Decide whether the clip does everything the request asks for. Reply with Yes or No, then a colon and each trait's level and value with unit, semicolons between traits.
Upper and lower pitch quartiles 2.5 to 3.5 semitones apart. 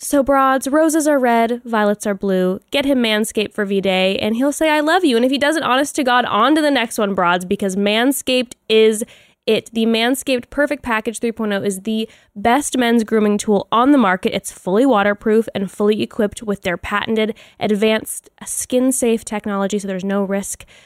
No: average, 4.1 semitones